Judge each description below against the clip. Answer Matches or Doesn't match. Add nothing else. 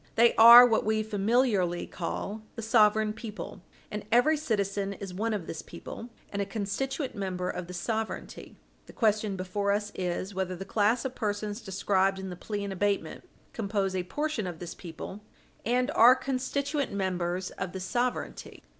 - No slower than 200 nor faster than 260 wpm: Doesn't match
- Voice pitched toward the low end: Doesn't match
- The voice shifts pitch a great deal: Doesn't match